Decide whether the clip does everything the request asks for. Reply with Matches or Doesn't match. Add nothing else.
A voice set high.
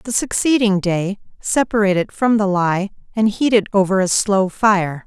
Matches